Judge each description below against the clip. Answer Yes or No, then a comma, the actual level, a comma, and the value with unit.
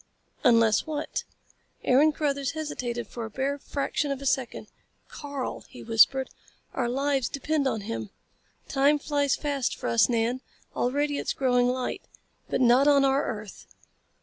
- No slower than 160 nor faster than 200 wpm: No, average, 150 wpm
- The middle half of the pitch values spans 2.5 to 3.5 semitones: Yes, average, 3.0 semitones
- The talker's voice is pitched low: No, very high, 265 Hz